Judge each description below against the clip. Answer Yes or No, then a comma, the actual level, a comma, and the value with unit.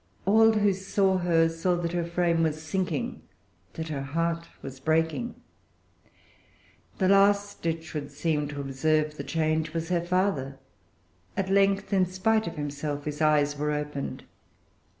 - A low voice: No, medium, 165 Hz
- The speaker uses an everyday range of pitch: Yes, average, 4.1 semitones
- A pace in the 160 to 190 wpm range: No, average, 150 wpm